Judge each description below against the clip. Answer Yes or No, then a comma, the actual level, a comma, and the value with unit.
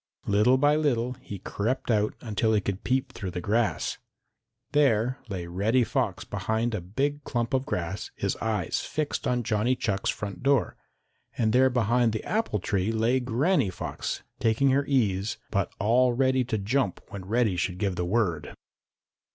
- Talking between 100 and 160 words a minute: No, average, 170 wpm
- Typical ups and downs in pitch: Yes, average, 4.3 semitones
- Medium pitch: No, low, 115 Hz